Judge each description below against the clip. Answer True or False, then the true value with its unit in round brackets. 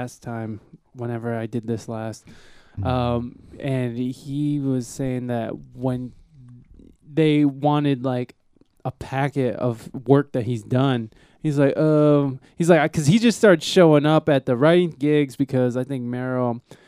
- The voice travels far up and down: False (3.2 semitones)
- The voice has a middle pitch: False (130 Hz)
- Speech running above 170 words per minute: False (150 wpm)